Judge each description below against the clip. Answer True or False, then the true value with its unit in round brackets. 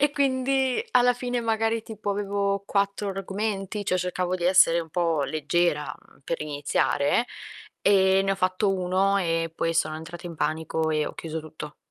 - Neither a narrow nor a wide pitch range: True (4.1 semitones)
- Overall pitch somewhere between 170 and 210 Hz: True (185 Hz)